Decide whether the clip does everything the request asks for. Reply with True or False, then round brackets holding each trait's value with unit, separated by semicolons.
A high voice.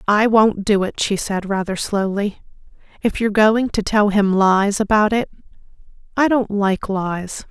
True (205 Hz)